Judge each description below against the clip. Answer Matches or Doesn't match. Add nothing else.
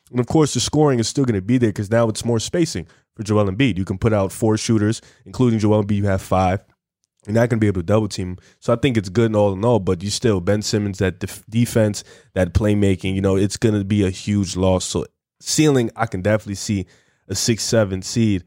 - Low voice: Matches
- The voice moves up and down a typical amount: Matches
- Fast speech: Matches